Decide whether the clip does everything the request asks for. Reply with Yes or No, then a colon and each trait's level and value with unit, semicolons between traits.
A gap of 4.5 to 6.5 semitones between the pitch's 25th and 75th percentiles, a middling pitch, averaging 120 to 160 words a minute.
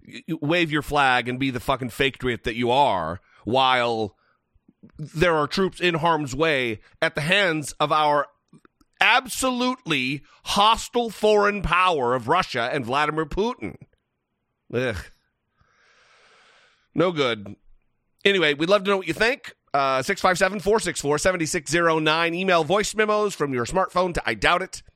Yes: wide, 5.4 semitones; medium, 160 Hz; average, 140 wpm